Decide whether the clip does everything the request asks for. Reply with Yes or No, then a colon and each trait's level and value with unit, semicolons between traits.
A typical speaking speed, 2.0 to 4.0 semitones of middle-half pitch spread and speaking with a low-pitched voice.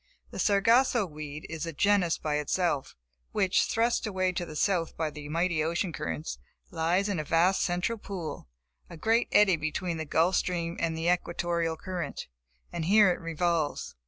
No: average, 170 wpm; average, 3.1 semitones; medium, 170 Hz